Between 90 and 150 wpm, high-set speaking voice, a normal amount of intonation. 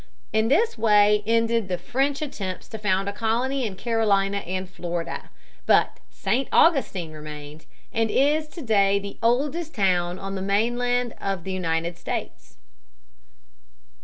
Yes: average, 140 wpm; high, 205 Hz; average, 4.5 semitones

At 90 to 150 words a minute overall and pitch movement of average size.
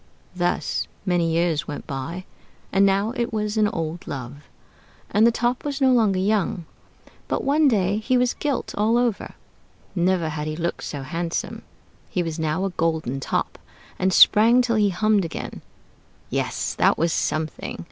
No: average, 165 wpm; average, 5.0 semitones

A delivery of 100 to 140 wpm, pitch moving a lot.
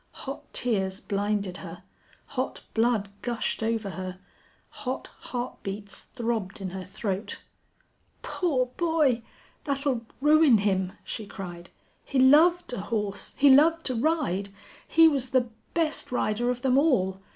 Yes: slow, 135 wpm; wide, 5.7 semitones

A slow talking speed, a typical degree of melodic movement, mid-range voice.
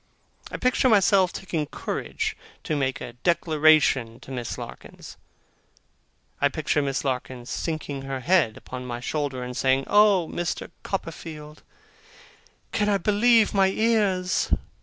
No: slow, 130 wpm; wide, 6.4 semitones; medium, 155 Hz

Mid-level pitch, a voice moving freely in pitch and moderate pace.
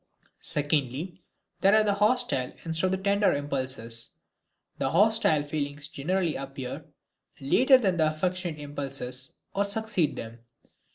No: medium, 155 Hz; wide, 6.1 semitones; slow, 125 wpm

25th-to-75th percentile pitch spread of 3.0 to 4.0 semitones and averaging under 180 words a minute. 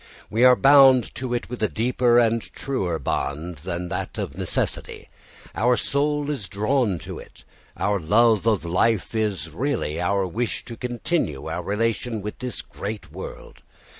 No: average, 4.8 semitones; average, 160 wpm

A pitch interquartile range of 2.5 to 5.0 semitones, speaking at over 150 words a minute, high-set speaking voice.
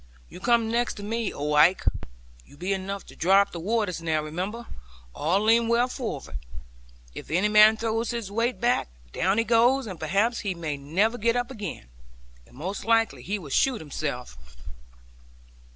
No: wide, 5.5 semitones; average, 175 wpm; high, 205 Hz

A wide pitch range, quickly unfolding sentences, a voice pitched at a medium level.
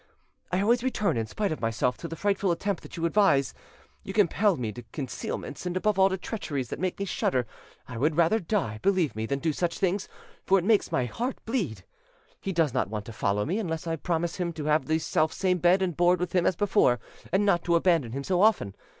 Yes: wide, 5.9 semitones; fast, 230 wpm; medium, 175 Hz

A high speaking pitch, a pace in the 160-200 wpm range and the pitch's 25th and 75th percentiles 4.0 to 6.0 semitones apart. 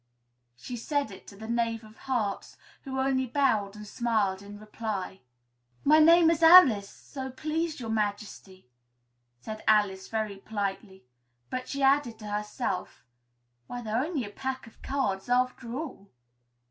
No: high, 225 Hz; average, 145 wpm; average, 4.4 semitones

